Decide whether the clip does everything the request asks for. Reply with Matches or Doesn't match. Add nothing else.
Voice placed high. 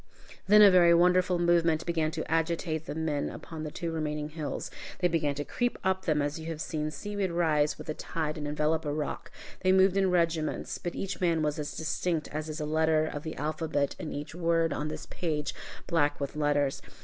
Doesn't match